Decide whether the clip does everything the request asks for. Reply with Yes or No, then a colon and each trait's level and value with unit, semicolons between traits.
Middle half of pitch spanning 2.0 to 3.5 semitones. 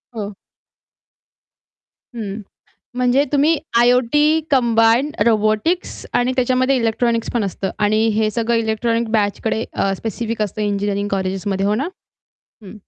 Yes: average, 2.9 semitones